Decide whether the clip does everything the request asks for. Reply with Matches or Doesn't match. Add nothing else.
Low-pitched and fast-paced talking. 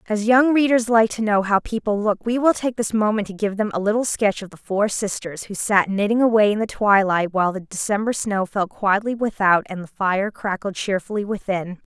Doesn't match